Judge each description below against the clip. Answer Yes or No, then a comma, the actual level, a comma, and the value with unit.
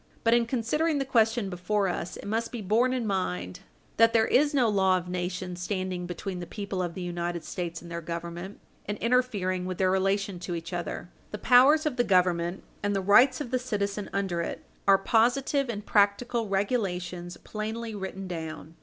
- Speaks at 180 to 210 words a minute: Yes, average, 190 wpm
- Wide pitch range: No, average, 4.4 semitones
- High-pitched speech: Yes, high, 195 Hz